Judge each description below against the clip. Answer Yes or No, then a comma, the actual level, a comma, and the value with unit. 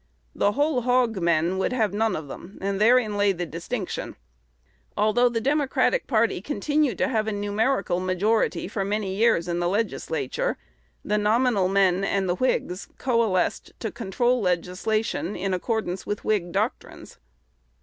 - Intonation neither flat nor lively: Yes, average, 4.1 semitones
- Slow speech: No, average, 150 wpm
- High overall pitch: Yes, high, 210 Hz